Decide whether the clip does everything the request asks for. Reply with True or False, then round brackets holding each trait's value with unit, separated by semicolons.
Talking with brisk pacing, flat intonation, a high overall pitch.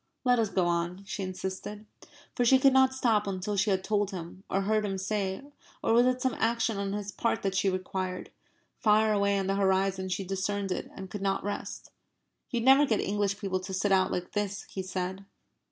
True (210 wpm; 2.1 semitones; 200 Hz)